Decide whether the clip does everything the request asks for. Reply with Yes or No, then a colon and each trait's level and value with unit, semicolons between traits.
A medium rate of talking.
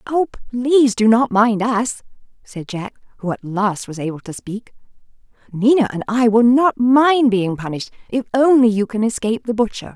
Yes: average, 180 wpm